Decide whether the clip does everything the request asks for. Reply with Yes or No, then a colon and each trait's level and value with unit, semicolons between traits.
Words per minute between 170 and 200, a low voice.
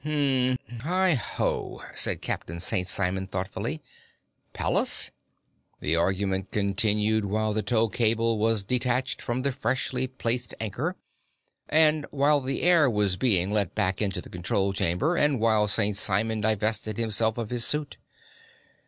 No: average, 140 wpm; low, 110 Hz